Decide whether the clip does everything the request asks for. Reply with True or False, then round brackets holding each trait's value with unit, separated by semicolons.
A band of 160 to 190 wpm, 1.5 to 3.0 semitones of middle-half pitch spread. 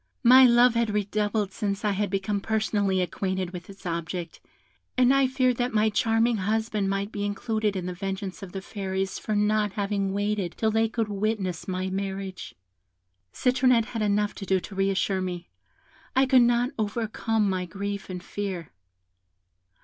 True (170 wpm; 2.5 semitones)